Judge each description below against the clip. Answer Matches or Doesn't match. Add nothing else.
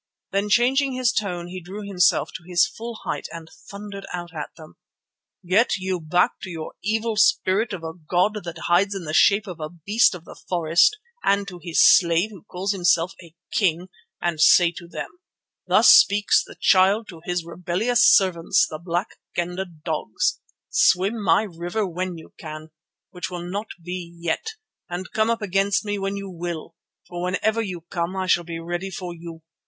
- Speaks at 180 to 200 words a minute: Matches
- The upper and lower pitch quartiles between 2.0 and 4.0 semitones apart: Matches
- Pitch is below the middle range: Doesn't match